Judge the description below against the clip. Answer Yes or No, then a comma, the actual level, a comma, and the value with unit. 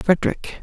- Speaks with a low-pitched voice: No, medium, 175 Hz